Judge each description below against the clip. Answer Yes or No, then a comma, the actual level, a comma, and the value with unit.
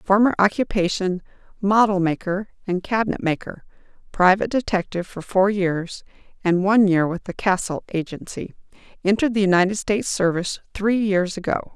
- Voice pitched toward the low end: No, high, 195 Hz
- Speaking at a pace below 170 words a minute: Yes, average, 140 wpm